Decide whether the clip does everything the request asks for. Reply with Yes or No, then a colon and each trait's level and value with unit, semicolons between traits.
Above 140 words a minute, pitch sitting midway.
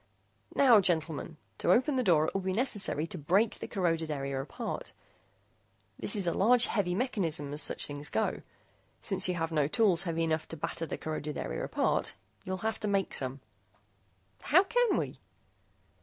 Yes: average, 175 wpm; medium, 175 Hz